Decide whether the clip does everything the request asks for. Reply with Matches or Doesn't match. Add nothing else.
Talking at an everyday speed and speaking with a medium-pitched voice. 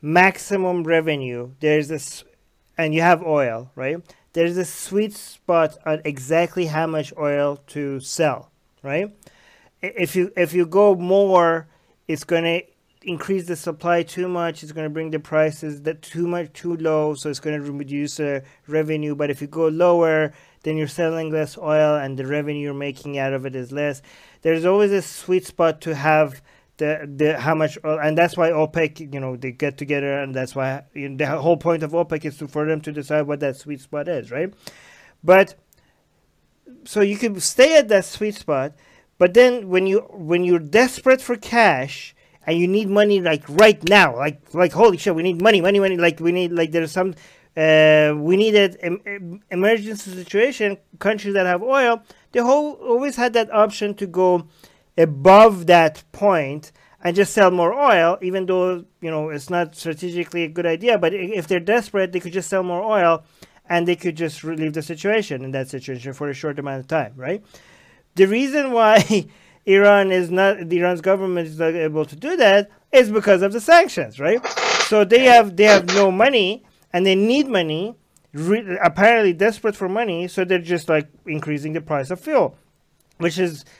Matches